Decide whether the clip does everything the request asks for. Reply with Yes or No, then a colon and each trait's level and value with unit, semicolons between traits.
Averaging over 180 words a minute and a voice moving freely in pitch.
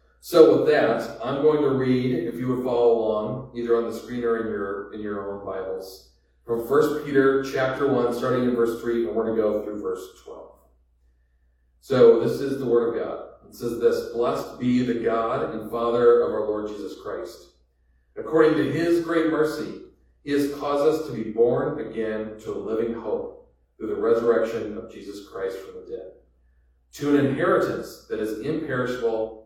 Yes: average, 190 wpm; wide, 5.7 semitones